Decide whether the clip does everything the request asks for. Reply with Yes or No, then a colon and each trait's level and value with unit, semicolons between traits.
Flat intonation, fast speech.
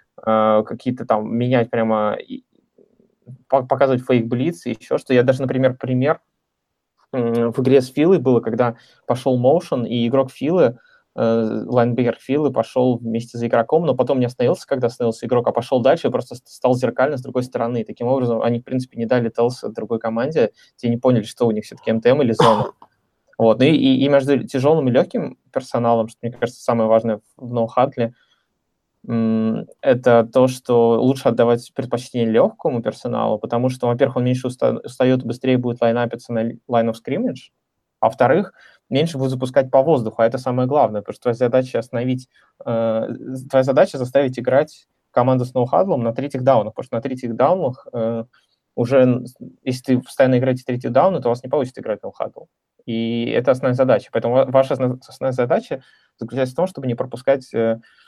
Yes: narrow, 2.1 semitones; fast, 175 wpm